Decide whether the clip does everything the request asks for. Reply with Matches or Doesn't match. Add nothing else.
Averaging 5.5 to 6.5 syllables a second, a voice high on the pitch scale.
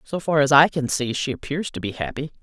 Doesn't match